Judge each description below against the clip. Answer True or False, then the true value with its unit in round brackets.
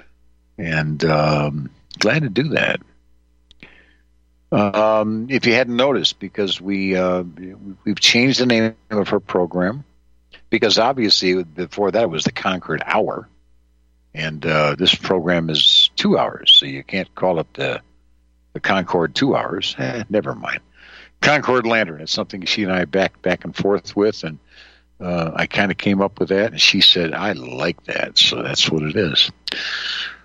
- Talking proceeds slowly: False (165 wpm)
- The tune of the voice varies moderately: False (8.3 semitones)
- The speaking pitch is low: True (90 Hz)